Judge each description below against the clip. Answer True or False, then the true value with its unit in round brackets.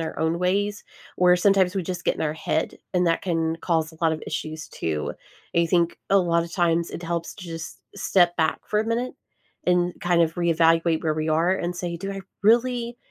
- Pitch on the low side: False (170 Hz)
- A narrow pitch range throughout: True (2.1 semitones)